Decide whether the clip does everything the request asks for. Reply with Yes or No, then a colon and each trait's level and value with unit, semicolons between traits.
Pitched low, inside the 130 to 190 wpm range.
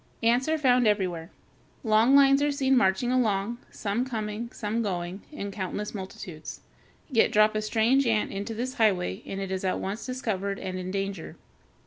No: high, 215 Hz; average, 170 wpm